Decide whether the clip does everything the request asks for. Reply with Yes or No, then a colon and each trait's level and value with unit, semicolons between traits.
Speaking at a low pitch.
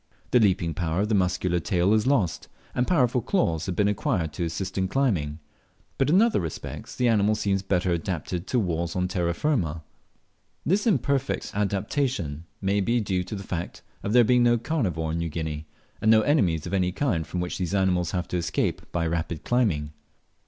Yes: very low, 95 Hz